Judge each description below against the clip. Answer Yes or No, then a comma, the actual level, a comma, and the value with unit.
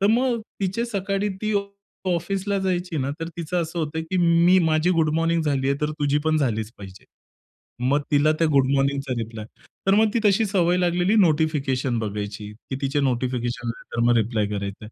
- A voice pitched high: No, medium, 155 Hz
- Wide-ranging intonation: Yes, wide, 5.9 semitones